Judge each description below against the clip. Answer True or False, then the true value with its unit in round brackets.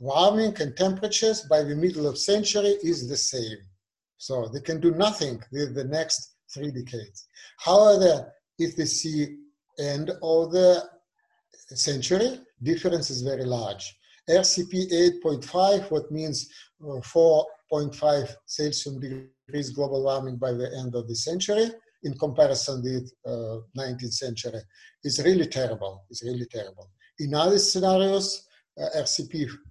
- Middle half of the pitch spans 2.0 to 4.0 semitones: False (5.5 semitones)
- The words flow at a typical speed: False (130 wpm)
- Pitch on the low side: False (150 Hz)